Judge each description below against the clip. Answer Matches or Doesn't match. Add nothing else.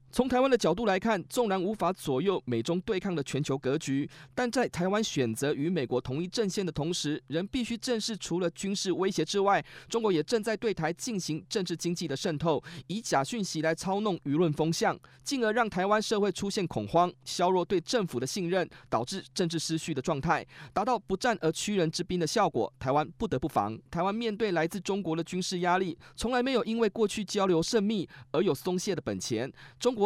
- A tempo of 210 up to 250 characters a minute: Doesn't match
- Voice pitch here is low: Doesn't match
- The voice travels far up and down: Doesn't match